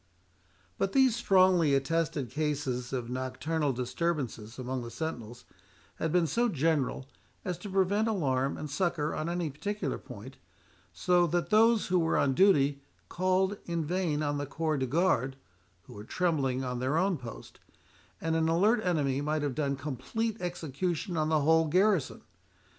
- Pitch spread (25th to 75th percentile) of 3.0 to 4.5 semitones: No, average, 4.9 semitones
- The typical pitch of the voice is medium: Yes, medium, 155 Hz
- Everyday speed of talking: Yes, average, 160 wpm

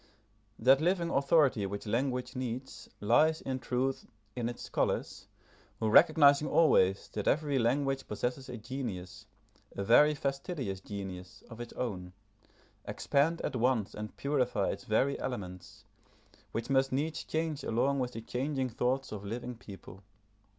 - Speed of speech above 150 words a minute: No, average, 140 wpm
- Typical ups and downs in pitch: Yes, average, 4.4 semitones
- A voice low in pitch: Yes, low, 125 Hz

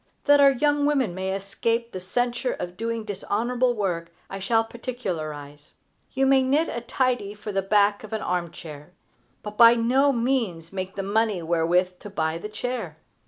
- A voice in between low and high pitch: No, high, 210 Hz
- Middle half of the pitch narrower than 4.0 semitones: No, average, 5.0 semitones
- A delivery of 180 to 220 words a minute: No, average, 170 wpm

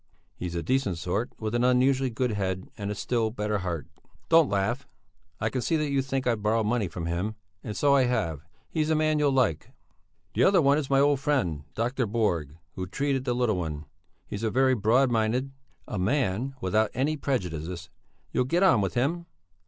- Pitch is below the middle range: Yes, low, 120 Hz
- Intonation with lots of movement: Yes, wide, 5.8 semitones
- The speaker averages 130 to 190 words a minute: No, average, 200 wpm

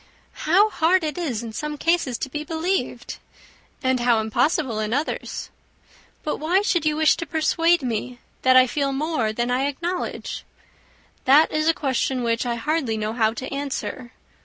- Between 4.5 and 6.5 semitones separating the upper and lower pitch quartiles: Yes, average, 4.8 semitones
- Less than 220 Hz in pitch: No, very high, 280 Hz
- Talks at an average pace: Yes, average, 170 wpm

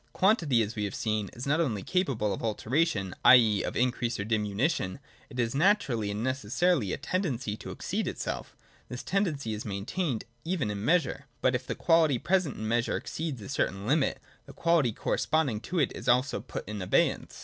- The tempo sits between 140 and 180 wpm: No, average, 195 wpm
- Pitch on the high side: No, low, 125 Hz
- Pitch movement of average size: No, wide, 6.7 semitones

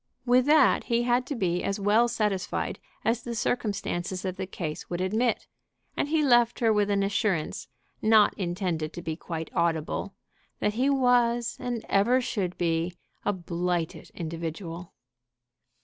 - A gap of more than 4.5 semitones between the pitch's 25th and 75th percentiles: Yes, wide, 5.5 semitones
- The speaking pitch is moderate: No, high, 200 Hz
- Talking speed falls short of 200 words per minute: Yes, average, 150 wpm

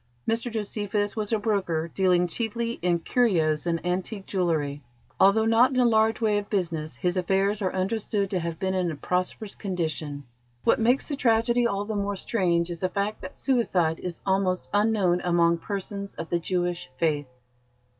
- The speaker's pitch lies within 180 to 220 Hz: Yes, high, 190 Hz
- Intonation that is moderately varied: Yes, average, 4.0 semitones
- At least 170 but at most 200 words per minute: Yes, average, 175 wpm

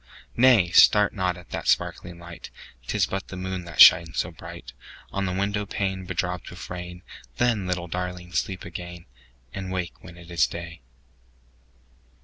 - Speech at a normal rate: Yes, average, 165 wpm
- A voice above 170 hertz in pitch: No, very low, 90 Hz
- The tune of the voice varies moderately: No, narrow, 1.6 semitones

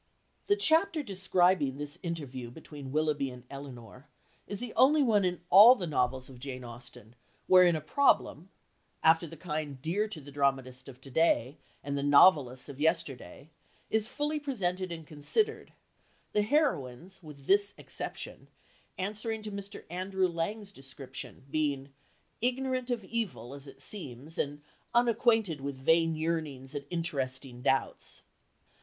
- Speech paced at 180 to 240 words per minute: No, average, 145 wpm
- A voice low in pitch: No, medium, 160 Hz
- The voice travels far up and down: Yes, wide, 6.8 semitones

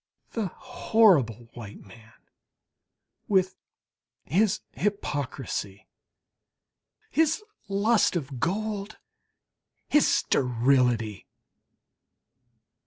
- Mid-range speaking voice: Yes, medium, 170 Hz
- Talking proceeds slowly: Yes, slow, 60 wpm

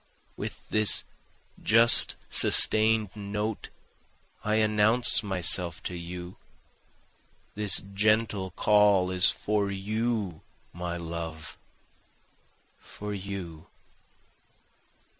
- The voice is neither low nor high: No, low, 100 Hz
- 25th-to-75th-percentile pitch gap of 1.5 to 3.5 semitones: Yes, average, 3.2 semitones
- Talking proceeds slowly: Yes, slow, 80 wpm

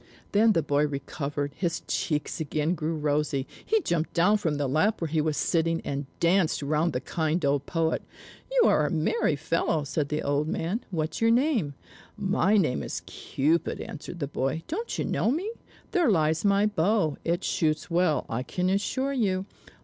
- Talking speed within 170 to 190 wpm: Yes, average, 180 wpm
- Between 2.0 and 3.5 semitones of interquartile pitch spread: No, average, 4.8 semitones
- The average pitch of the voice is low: No, medium, 160 Hz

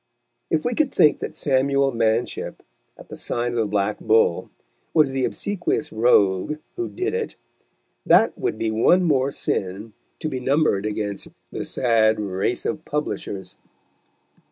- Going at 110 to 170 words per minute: Yes, average, 150 wpm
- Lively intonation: Yes, wide, 6.2 semitones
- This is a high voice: No, low, 125 Hz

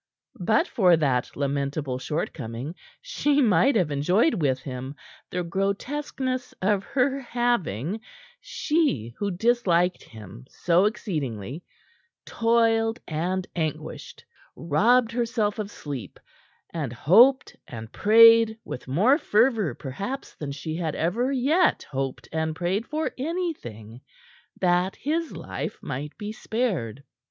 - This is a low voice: No, medium, 185 Hz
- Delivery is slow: Yes, slow, 115 wpm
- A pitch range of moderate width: No, wide, 8.6 semitones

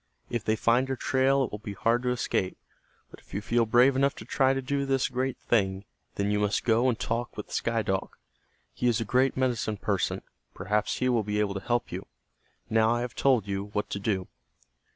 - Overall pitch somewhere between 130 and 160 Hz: No, low, 115 Hz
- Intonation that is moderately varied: Yes, average, 3.6 semitones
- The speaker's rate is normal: No, fast, 220 wpm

